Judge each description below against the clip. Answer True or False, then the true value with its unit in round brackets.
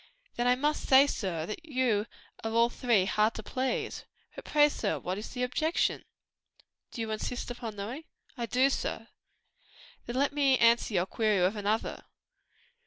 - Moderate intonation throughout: True (3.7 semitones)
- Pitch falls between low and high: False (235 Hz)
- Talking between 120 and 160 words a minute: False (170 wpm)